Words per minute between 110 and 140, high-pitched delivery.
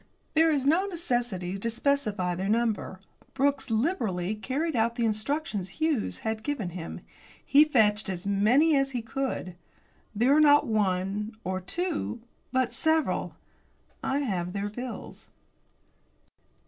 Yes: slow, 135 wpm; high, 235 Hz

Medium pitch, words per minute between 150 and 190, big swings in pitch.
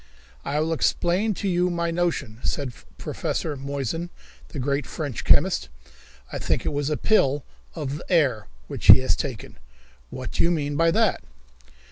No: medium, 150 Hz; average, 165 wpm; average, 3.7 semitones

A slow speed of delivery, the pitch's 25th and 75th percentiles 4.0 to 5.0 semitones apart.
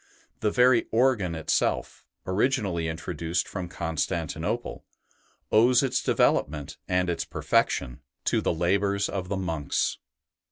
Yes: slow, 115 wpm; average, 4.3 semitones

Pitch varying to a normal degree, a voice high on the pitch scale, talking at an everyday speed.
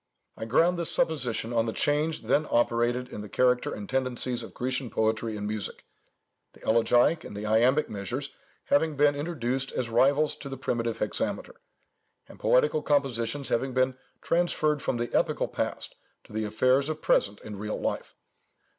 No: average, 4.1 semitones; low, 125 Hz; average, 165 wpm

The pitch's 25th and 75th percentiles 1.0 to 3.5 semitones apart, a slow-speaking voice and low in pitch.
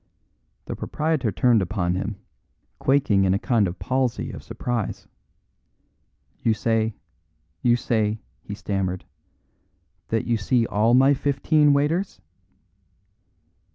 No: average, 4.6 semitones; slow, 115 wpm; low, 115 Hz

